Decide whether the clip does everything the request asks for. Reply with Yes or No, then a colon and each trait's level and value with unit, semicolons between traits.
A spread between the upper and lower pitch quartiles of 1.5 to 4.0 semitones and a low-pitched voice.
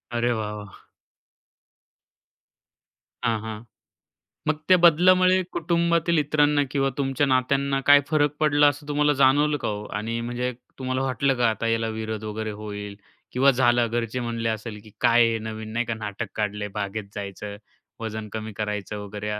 No: average, 4.9 semitones; low, 120 Hz